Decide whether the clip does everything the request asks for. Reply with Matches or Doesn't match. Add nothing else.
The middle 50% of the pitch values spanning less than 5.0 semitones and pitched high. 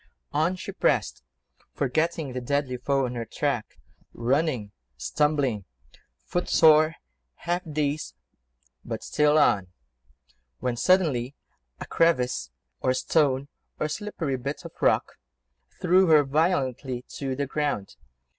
Doesn't match